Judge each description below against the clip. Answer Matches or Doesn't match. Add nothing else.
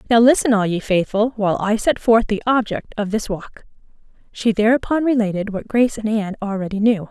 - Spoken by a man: Doesn't match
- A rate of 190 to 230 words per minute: Matches